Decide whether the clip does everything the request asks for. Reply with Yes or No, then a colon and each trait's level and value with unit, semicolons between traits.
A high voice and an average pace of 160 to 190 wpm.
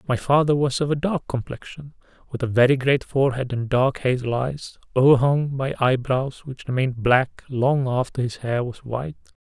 No: low, 130 Hz; average, 180 wpm